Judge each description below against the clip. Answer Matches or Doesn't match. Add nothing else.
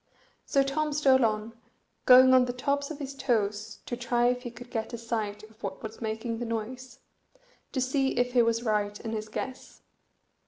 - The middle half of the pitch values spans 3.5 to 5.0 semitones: Doesn't match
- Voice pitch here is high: Matches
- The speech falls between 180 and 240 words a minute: Matches